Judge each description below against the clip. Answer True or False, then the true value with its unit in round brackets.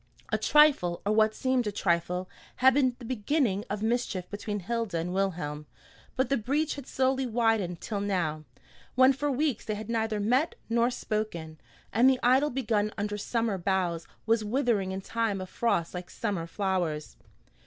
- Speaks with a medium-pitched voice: False (215 Hz)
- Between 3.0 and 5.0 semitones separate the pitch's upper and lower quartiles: True (4.7 semitones)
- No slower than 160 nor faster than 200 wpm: True (170 wpm)